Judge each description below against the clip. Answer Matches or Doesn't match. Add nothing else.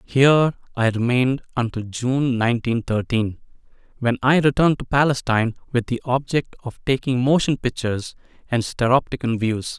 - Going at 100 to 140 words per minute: Matches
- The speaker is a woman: Doesn't match